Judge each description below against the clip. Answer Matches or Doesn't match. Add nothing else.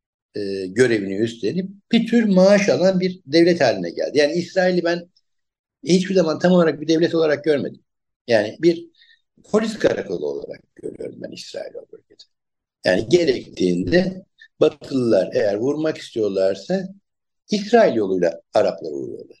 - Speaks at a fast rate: Doesn't match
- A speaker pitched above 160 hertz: Matches